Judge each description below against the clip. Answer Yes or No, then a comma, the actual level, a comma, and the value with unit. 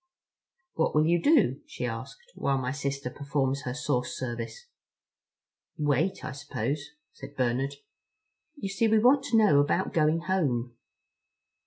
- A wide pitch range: Yes, wide, 5.7 semitones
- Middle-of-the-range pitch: Yes, medium, 145 Hz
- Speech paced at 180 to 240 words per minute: No, average, 140 wpm